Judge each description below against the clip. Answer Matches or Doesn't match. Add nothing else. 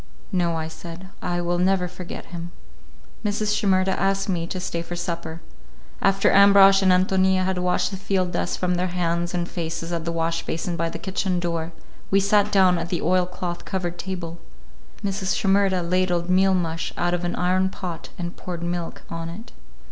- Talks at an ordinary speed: Matches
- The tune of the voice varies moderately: Doesn't match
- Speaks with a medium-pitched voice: Matches